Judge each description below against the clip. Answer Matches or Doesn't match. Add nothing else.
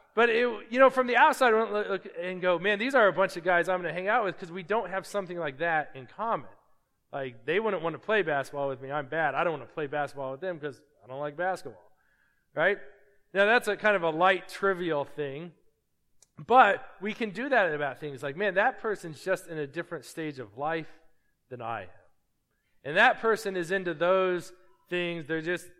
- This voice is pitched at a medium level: Matches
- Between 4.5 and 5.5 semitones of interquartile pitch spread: Matches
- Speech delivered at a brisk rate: Matches